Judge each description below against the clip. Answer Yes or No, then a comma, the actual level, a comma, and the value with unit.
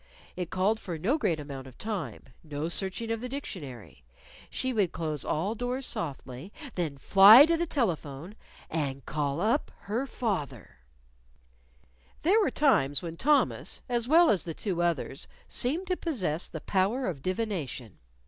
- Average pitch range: No, wide, 8.3 semitones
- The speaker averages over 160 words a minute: No, average, 155 wpm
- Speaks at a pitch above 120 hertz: Yes, medium, 185 Hz